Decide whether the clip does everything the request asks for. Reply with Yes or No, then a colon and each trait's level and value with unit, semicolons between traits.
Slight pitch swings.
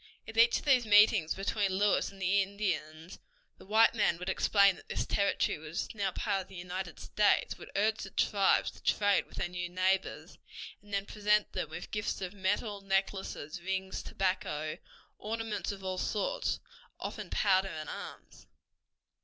Yes: narrow, 2.1 semitones